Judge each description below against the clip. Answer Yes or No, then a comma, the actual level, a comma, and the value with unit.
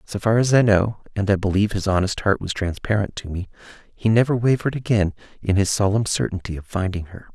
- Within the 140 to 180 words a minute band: No, average, 195 wpm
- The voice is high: No, low, 100 Hz